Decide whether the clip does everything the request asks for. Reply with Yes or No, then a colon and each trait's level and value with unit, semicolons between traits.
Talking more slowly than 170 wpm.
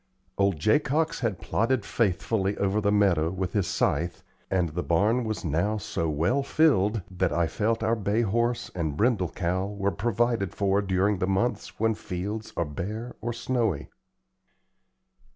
Yes: average, 155 wpm